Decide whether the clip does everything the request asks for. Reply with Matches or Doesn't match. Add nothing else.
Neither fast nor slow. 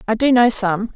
Doesn't match